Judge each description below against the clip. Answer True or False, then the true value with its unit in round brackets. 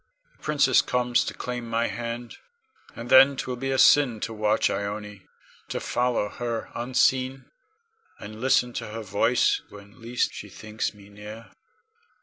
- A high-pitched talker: False (115 Hz)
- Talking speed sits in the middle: True (150 wpm)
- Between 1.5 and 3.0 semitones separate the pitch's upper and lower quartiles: True (2.7 semitones)